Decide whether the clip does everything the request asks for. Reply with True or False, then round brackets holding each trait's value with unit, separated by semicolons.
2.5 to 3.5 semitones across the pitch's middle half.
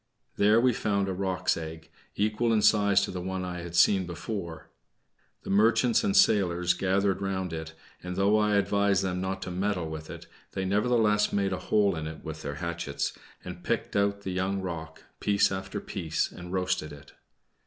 True (2.8 semitones)